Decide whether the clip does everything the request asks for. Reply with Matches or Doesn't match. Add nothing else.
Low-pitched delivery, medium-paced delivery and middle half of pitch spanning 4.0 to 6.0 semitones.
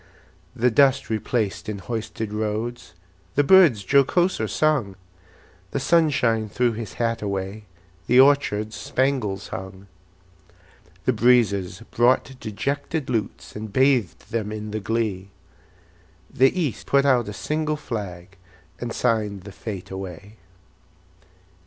Doesn't match